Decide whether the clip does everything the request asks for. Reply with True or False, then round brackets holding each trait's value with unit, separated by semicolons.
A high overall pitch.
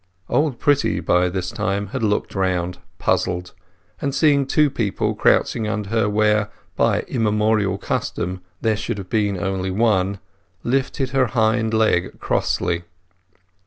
False (105 Hz)